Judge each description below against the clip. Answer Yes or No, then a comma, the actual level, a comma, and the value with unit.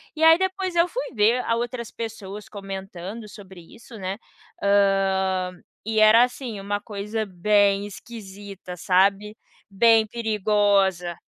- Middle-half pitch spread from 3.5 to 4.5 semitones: No, average, 2.8 semitones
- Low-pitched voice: No, high, 205 Hz